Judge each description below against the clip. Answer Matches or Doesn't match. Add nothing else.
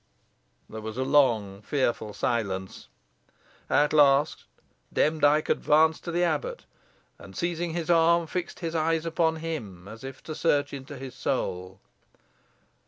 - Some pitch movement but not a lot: Doesn't match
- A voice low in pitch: Doesn't match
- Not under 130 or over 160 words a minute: Matches